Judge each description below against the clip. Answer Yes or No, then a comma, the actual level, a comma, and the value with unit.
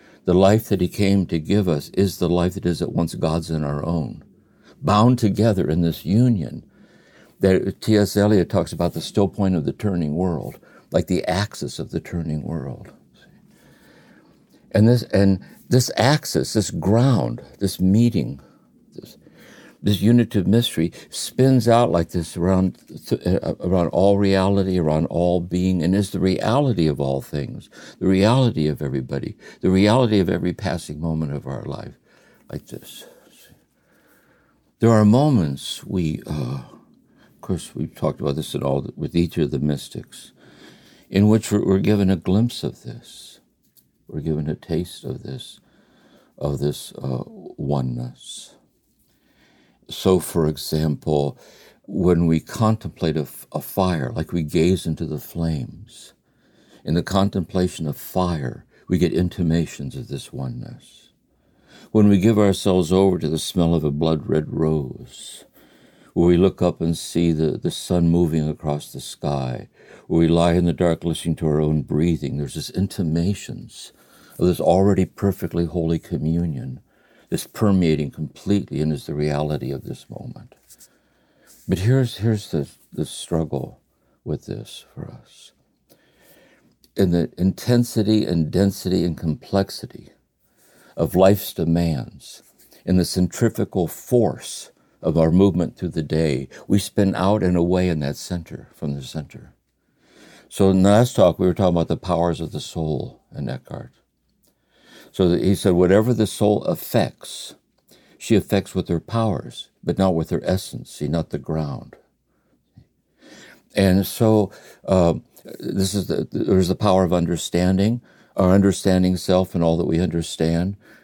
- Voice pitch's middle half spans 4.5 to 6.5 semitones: No, average, 3.7 semitones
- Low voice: Yes, very low, 90 Hz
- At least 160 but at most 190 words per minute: No, average, 150 wpm